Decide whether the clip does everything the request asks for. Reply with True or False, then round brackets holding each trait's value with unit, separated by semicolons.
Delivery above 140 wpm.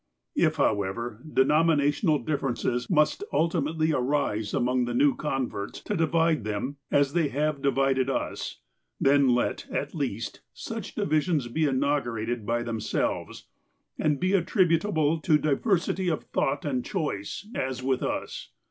False (135 wpm)